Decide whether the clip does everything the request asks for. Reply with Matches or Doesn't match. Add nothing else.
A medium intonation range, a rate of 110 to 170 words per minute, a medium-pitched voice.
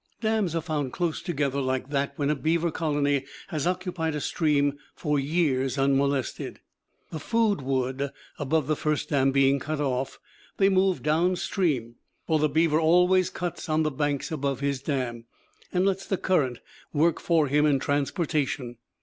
Matches